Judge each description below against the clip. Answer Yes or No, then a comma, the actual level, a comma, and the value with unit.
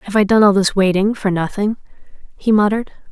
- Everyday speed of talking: Yes, average, 195 wpm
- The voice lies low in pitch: No, high, 205 Hz